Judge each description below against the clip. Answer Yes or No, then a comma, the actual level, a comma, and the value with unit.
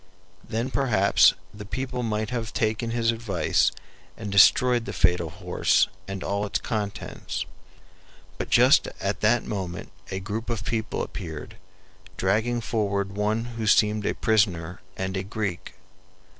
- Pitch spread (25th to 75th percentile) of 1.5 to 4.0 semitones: Yes, average, 2.8 semitones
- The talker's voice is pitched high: No, low, 105 Hz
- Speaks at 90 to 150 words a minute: Yes, average, 140 wpm